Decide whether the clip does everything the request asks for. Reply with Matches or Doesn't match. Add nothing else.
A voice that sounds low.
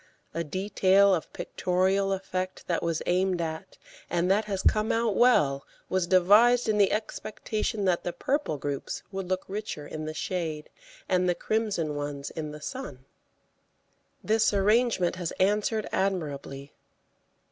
Doesn't match